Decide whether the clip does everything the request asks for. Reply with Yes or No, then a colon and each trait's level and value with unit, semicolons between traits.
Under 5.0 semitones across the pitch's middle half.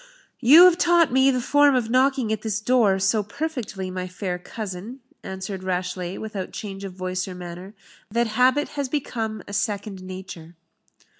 No: average, 5.3 semitones